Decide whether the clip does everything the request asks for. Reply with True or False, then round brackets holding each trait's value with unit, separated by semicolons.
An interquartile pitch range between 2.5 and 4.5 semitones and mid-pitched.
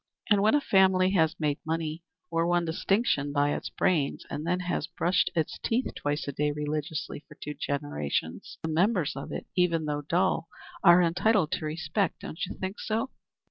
True (3.8 semitones; 165 Hz)